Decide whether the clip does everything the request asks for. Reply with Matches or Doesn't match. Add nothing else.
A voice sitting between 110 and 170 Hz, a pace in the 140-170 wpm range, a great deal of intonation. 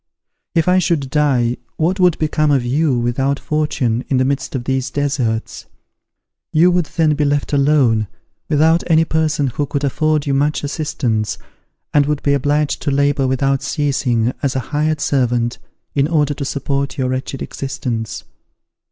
Doesn't match